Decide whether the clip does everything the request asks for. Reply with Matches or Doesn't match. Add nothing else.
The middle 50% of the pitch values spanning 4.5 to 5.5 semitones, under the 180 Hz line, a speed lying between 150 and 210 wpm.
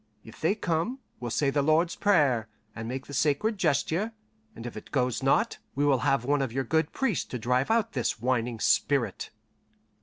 Matches